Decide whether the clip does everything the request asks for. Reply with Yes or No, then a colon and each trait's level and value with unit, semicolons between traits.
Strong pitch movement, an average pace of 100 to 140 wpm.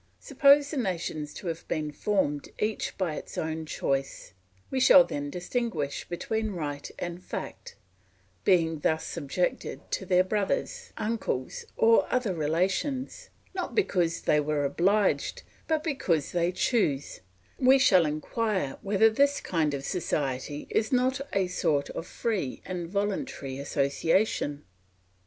Yes: wide, 6.8 semitones; slow, 135 wpm